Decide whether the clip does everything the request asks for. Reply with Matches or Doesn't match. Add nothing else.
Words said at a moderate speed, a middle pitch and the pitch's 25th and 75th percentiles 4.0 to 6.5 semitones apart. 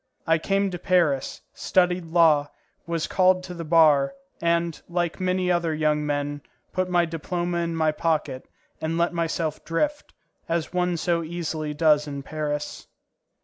Doesn't match